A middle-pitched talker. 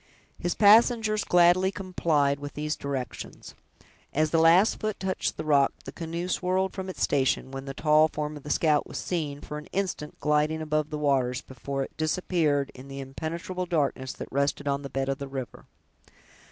Yes: medium, 150 Hz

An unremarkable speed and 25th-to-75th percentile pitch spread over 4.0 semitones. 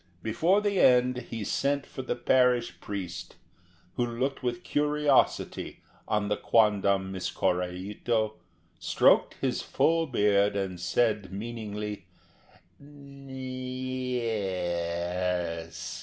No: slow, 105 wpm; average, 5.2 semitones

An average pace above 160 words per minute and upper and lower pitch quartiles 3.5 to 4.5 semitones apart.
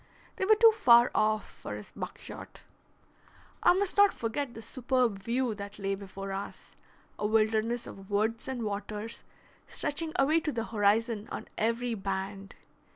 No: average, 155 wpm; average, 3.8 semitones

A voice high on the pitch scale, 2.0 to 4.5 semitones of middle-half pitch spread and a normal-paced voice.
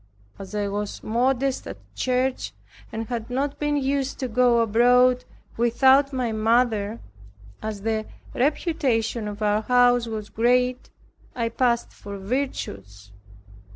No: high, 240 Hz; average, 2.9 semitones; slow, 125 wpm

